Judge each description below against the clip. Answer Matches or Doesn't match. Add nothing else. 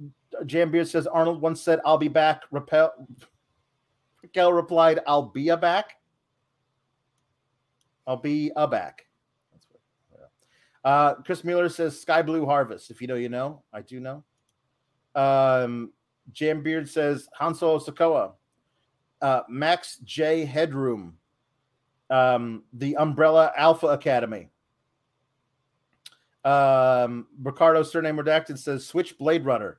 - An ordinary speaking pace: Doesn't match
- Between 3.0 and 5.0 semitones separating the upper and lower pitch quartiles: Matches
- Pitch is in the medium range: Matches